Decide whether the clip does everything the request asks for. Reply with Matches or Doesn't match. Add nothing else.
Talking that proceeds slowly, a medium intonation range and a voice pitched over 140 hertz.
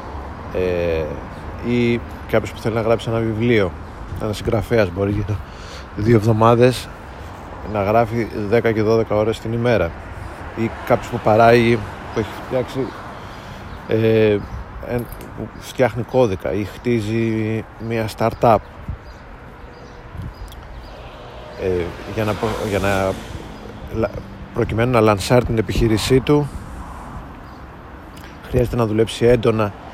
Doesn't match